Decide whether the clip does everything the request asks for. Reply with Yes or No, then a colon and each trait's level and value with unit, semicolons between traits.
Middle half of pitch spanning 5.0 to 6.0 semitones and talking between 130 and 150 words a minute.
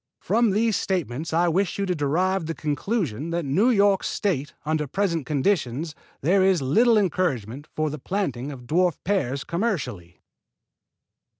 Yes: wide, 5.4 semitones; average, 140 wpm